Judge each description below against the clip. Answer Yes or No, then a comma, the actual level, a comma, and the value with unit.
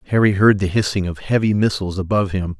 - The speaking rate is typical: No, fast, 210 wpm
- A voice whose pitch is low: Yes, very low, 95 Hz